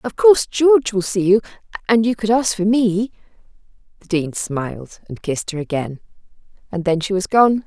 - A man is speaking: No, female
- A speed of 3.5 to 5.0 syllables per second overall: No, 5.4 syllables/s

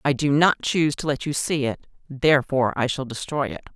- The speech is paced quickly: Yes, fast, 225 wpm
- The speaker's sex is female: Yes, female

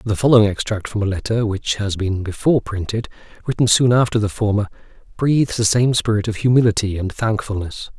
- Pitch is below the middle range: Yes, low, 110 Hz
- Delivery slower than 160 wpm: No, average, 180 wpm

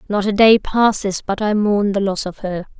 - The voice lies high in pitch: Yes, high, 205 Hz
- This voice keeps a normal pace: No, fast, 235 wpm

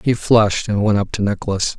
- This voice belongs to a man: Yes, male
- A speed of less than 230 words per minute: No, fast, 235 wpm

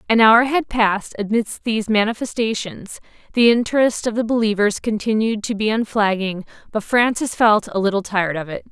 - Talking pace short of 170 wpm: Yes, average, 160 wpm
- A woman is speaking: Yes, female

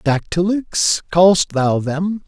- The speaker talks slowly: Yes, slow, 105 wpm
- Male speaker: Yes, male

